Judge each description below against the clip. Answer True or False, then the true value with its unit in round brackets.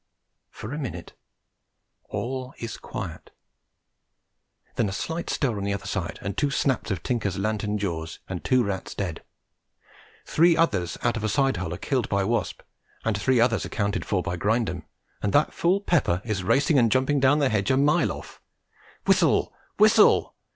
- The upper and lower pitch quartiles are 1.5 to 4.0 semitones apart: False (5.3 semitones)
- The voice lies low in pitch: True (115 Hz)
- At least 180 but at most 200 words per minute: False (170 wpm)